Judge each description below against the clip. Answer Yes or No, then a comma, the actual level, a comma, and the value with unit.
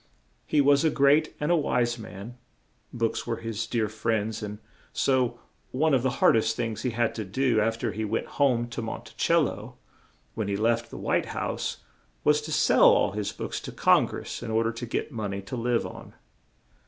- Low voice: Yes, low, 115 Hz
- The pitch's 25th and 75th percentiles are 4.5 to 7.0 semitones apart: No, average, 3.0 semitones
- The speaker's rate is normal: No, fast, 215 wpm